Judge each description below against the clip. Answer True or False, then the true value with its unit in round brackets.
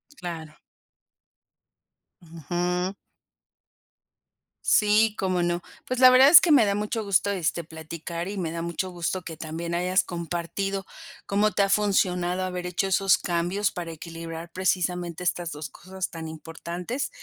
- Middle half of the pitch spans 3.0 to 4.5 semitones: False (2.6 semitones)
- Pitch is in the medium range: True (180 Hz)